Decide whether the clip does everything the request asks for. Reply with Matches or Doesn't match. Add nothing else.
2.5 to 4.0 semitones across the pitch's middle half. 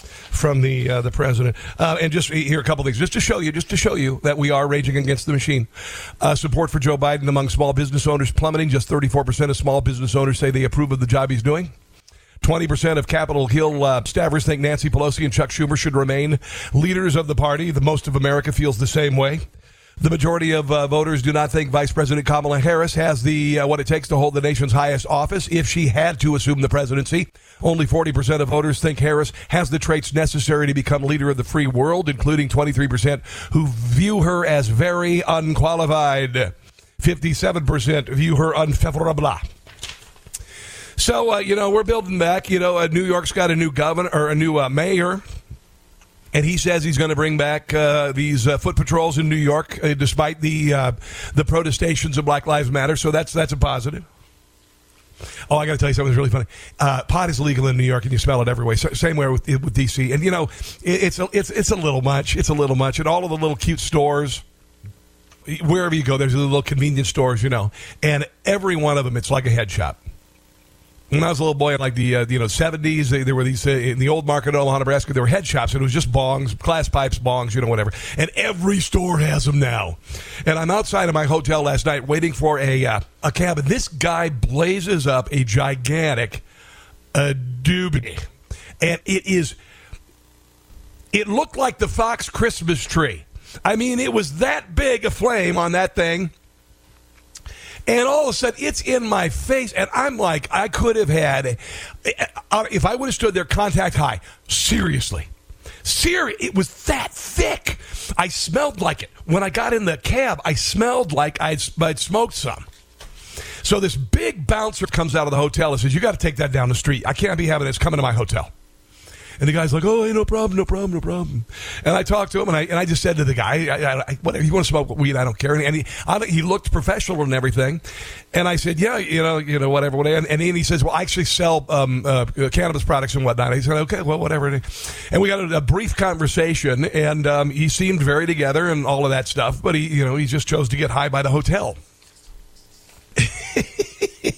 Matches